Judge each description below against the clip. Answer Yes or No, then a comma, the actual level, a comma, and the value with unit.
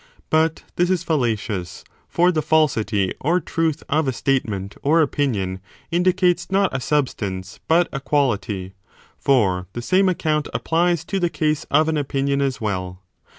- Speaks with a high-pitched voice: No, medium, 145 Hz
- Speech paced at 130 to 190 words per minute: Yes, average, 150 wpm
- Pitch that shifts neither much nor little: No, wide, 7.2 semitones